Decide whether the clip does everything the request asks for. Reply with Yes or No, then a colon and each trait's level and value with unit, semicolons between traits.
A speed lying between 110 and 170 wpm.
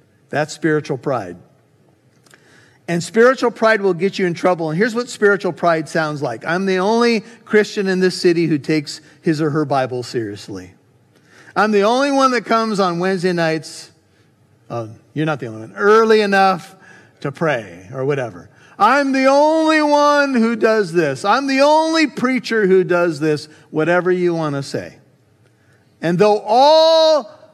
Yes: average, 165 wpm